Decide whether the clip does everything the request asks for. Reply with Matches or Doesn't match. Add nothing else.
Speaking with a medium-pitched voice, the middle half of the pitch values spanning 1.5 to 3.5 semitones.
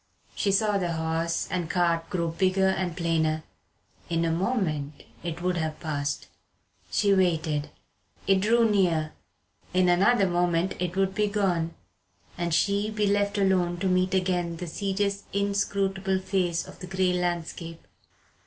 Matches